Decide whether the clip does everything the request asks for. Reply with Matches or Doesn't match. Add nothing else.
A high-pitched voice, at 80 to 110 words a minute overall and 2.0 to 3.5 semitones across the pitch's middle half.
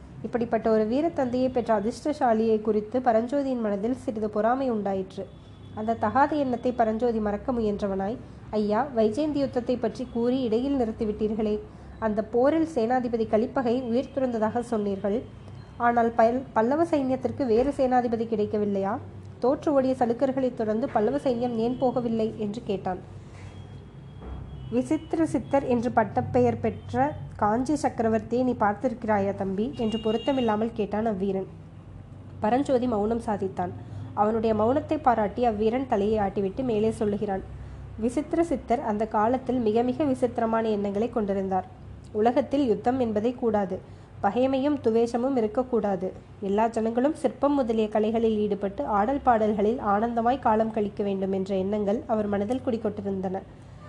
Doesn't match